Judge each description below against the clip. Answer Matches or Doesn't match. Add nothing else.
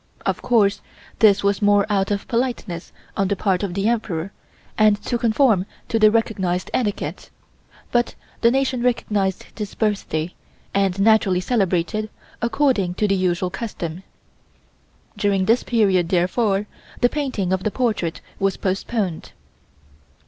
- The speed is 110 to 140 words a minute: Matches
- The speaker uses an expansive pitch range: Doesn't match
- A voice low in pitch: Doesn't match